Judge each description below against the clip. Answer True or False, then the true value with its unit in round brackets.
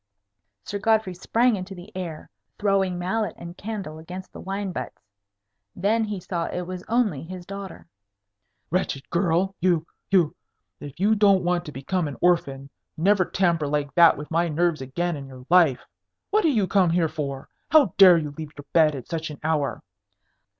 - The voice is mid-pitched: True (175 Hz)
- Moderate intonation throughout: True (3.8 semitones)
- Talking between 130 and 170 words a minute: False (180 wpm)